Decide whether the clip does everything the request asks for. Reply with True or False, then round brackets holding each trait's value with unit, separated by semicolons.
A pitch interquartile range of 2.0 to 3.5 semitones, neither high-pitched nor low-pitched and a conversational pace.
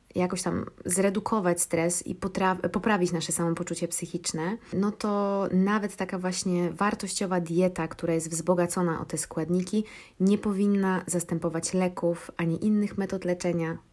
True (2.6 semitones; 180 Hz; 135 wpm)